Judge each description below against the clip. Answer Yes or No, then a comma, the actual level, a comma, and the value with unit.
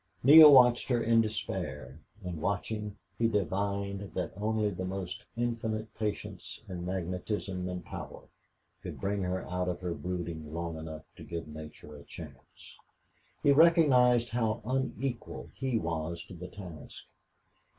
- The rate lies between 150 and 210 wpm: No, average, 140 wpm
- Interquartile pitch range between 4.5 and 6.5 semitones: Yes, average, 4.8 semitones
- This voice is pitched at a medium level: No, very low, 95 Hz